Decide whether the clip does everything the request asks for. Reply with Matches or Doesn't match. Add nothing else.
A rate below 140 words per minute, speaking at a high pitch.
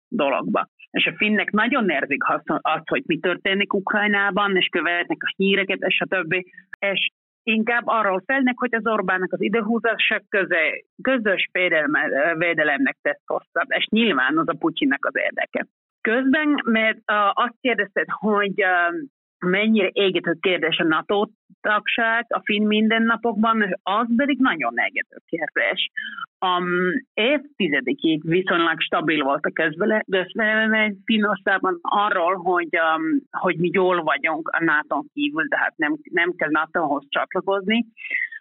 Matches